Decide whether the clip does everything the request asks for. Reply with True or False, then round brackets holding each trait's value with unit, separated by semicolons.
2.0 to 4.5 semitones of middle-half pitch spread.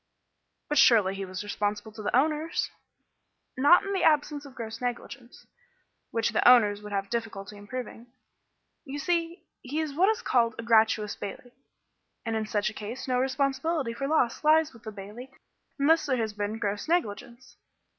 False (5.4 semitones)